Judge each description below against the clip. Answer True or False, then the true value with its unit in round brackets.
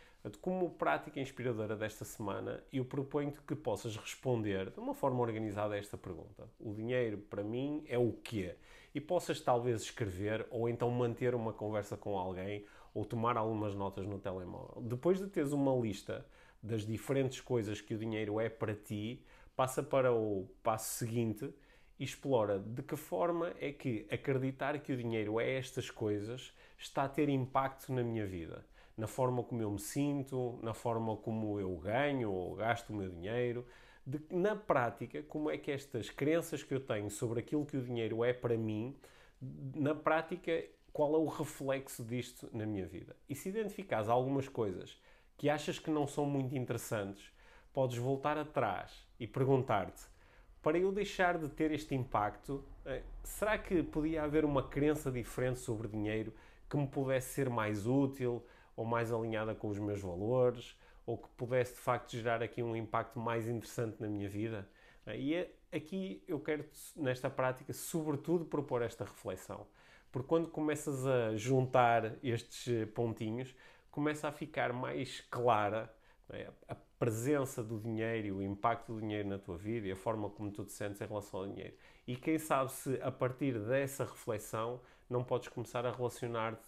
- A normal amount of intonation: True (4.3 semitones)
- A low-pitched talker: True (125 Hz)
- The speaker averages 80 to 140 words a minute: False (170 wpm)